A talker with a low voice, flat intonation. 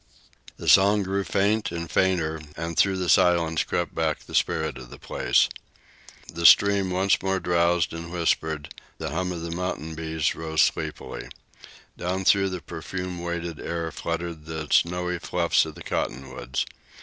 Yes: very low, 85 Hz; narrow, 2.2 semitones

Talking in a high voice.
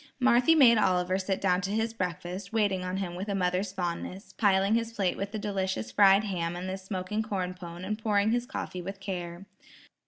Yes: high, 195 Hz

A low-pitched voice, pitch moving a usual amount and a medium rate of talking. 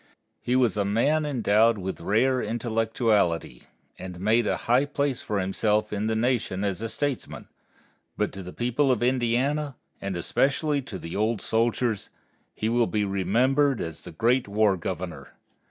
Yes: low, 110 Hz; average, 4.1 semitones; average, 160 wpm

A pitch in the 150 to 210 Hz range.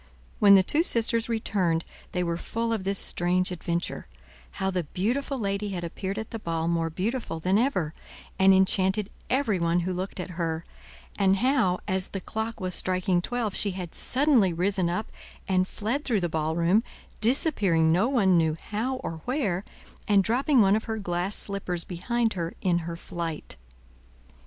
Yes: high, 190 Hz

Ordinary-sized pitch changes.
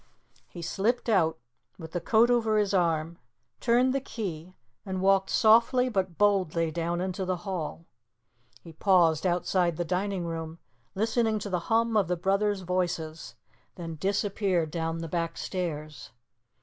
Yes: average, 3.6 semitones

